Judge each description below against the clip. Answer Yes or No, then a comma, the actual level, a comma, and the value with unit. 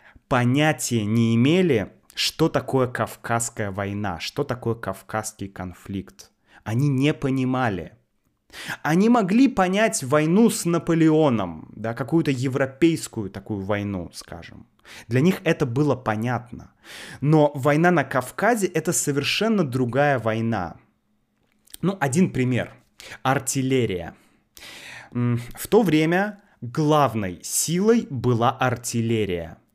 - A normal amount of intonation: No, wide, 5.9 semitones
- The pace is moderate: No, slow, 100 wpm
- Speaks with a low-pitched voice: Yes, low, 130 Hz